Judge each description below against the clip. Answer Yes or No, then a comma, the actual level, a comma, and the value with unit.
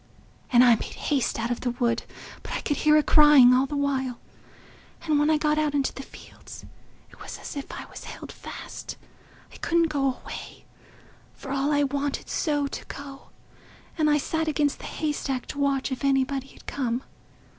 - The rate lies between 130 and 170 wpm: No, average, 190 wpm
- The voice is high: Yes, very high, 280 Hz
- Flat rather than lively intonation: Yes, narrow, 2.2 semitones